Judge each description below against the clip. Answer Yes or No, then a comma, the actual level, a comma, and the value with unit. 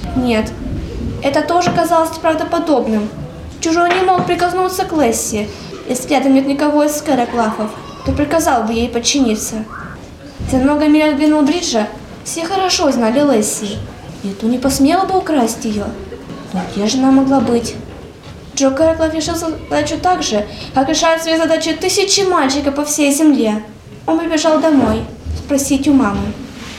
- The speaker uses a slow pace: No, average, 145 wpm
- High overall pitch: Yes, very high, 290 Hz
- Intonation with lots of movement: No, average, 5.0 semitones